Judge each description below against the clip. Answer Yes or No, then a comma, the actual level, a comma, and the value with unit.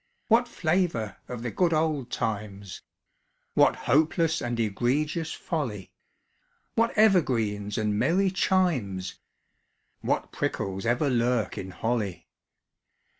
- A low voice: Yes, low, 125 Hz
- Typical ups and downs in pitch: No, wide, 7.8 semitones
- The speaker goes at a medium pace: No, slow, 110 wpm